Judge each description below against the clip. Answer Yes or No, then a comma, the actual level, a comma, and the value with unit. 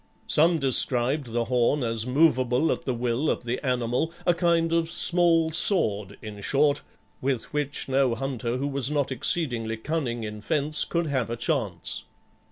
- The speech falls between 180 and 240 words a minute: No, average, 165 wpm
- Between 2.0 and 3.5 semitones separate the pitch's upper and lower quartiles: No, average, 4.7 semitones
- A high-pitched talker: No, low, 135 Hz